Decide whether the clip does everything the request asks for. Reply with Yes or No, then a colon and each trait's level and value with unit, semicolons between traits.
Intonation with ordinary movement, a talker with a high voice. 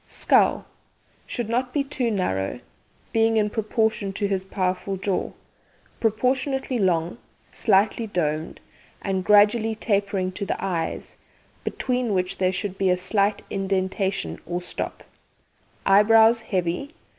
Yes: average, 3.2 semitones; high, 200 Hz